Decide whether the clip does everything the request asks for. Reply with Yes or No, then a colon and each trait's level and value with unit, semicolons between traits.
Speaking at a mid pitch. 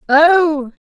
No: very high, 305 Hz